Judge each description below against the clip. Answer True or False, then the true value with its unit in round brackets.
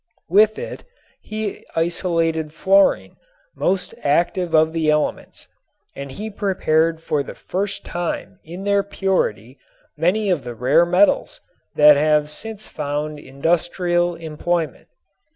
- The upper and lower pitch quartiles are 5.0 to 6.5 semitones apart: False (3.9 semitones)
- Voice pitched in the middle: True (165 Hz)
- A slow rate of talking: True (120 wpm)